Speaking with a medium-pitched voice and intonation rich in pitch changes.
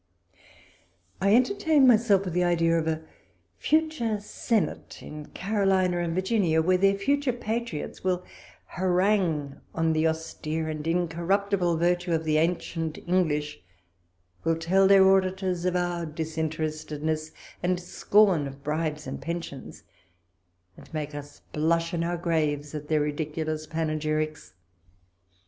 No: medium, 170 Hz; average, 3.4 semitones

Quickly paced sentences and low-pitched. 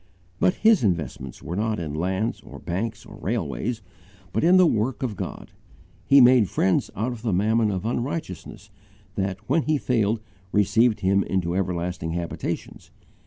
No: average, 160 wpm; low, 105 Hz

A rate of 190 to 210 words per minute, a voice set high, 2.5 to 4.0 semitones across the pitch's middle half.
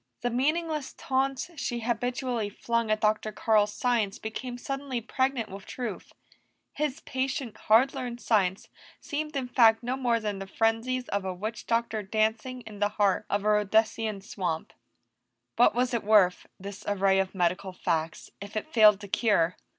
No: average, 165 wpm; high, 220 Hz; average, 3.6 semitones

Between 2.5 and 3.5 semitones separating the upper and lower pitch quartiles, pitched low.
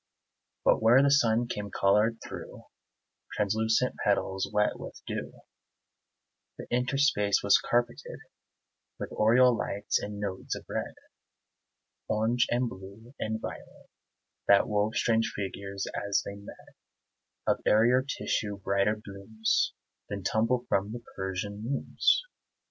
Yes: average, 2.9 semitones; low, 110 Hz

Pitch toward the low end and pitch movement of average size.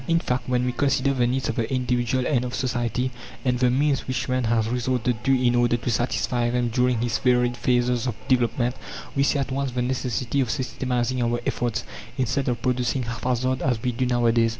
No: low, 125 Hz; narrow, 1.3 semitones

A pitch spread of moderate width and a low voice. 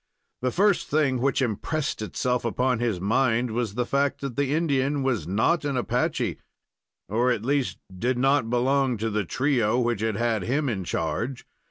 Yes: average, 3.5 semitones; low, 125 Hz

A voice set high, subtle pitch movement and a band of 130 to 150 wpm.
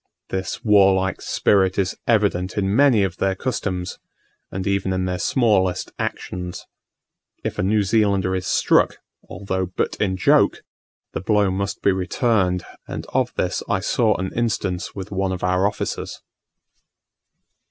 No: very low, 95 Hz; narrow, 1.7 semitones; average, 145 wpm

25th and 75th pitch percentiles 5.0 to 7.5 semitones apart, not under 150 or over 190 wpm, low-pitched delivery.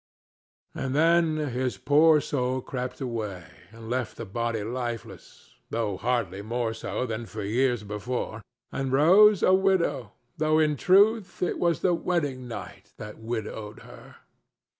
No: wide, 5.5 semitones; average, 140 wpm; low, 125 Hz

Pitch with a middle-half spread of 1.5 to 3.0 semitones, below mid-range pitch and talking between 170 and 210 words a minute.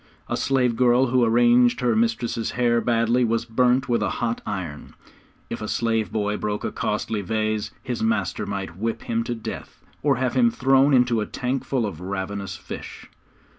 Yes: narrow, 2.5 semitones; low, 115 Hz; average, 180 wpm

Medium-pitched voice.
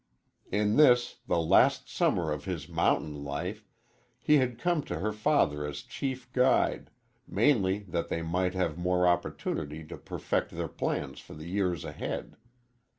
No: very low, 90 Hz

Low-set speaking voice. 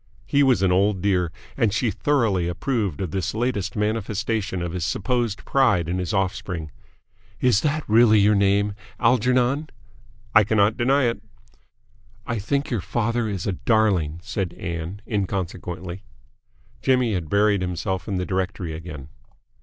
Yes: low, 100 Hz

